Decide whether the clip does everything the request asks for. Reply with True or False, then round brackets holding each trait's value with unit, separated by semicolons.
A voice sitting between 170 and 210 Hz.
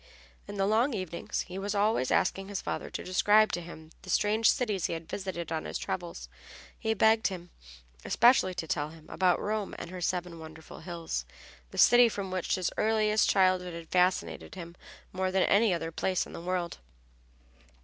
True (185 Hz)